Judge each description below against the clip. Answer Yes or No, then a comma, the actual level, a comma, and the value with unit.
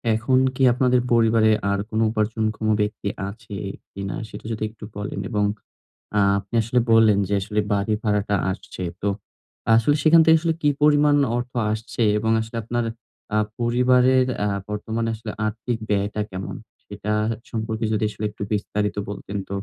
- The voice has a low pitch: Yes, low, 110 Hz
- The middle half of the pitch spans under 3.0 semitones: Yes, narrow, 2.5 semitones